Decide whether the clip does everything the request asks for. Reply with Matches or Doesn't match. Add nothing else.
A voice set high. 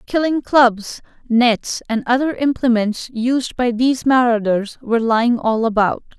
Matches